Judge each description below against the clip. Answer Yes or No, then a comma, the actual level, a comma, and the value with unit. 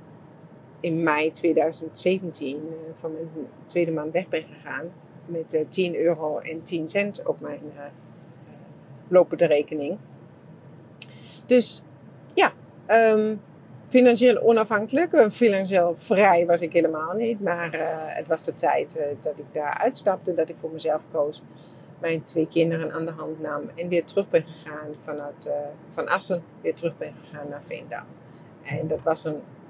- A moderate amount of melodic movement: No, narrow, 2.3 semitones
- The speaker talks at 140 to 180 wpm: Yes, average, 155 wpm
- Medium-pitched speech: Yes, medium, 160 Hz